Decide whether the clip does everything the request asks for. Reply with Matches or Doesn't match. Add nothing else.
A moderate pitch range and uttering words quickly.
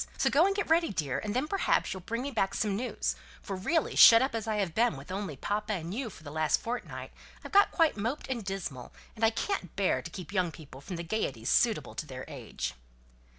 Doesn't match